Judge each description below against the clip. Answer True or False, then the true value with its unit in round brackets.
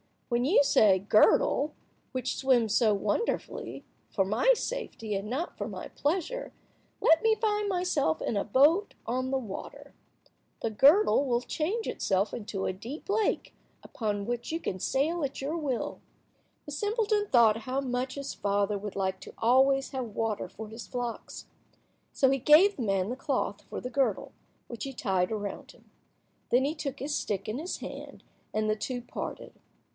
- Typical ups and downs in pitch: False (5.8 semitones)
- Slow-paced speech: False (170 wpm)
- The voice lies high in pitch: True (255 Hz)